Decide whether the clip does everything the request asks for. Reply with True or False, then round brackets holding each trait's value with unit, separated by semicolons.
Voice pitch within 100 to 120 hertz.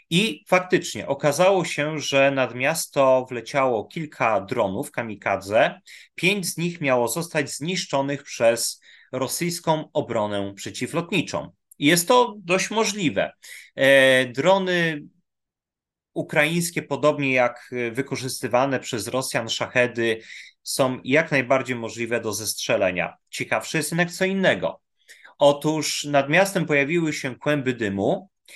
False (140 Hz)